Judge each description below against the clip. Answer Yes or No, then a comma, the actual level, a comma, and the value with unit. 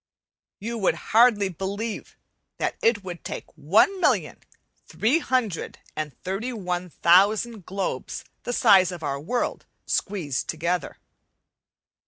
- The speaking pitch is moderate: No, high, 195 Hz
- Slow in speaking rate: Yes, slow, 120 wpm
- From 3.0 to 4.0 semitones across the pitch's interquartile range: No, average, 4.4 semitones